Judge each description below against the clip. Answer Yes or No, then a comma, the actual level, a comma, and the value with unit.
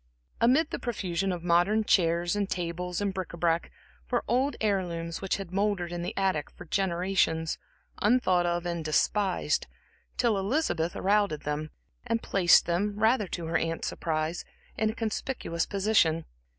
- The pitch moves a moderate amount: Yes, average, 3.6 semitones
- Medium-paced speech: Yes, average, 165 wpm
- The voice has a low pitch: No, medium, 185 Hz